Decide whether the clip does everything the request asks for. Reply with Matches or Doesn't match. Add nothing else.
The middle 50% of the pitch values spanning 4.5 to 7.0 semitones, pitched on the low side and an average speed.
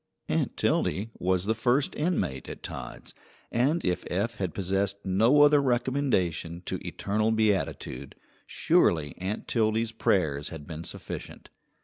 Doesn't match